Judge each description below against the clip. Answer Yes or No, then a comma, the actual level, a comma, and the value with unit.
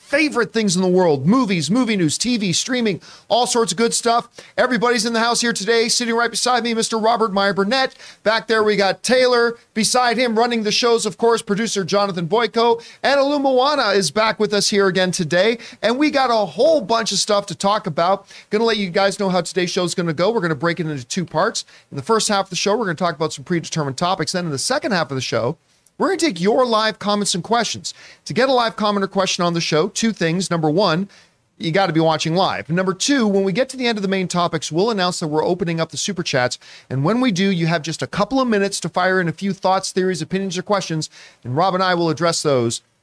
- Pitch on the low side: No, high, 200 Hz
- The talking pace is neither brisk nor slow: No, fast, 255 wpm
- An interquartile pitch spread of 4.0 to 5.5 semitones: Yes, average, 4.8 semitones